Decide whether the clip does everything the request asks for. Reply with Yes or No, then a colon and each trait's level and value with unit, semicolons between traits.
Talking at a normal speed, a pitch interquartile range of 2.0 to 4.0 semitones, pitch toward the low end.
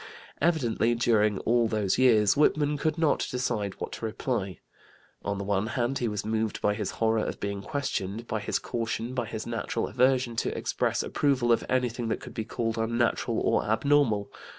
Yes: average, 180 wpm; average, 2.8 semitones; low, 115 Hz